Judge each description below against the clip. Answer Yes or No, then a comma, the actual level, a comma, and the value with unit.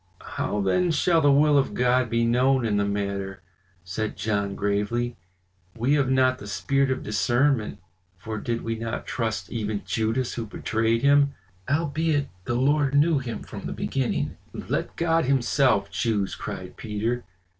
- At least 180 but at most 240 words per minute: No, average, 155 wpm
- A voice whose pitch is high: No, low, 120 Hz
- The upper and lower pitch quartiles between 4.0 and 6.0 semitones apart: Yes, average, 4.6 semitones